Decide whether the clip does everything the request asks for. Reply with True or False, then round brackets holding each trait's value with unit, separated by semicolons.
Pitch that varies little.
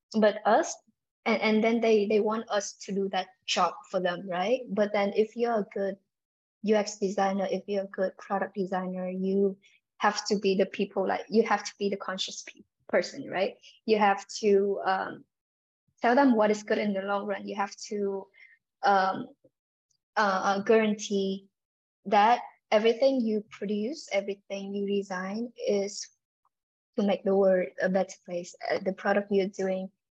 True (1.8 semitones)